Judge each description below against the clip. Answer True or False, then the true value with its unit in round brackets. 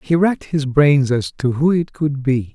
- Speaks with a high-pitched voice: False (140 Hz)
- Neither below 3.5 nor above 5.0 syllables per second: True (4.5 syllables/s)